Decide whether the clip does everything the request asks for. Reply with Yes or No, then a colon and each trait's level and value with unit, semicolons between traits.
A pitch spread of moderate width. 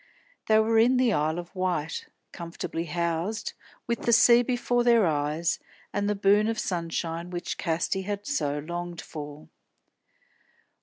Yes: average, 5.0 semitones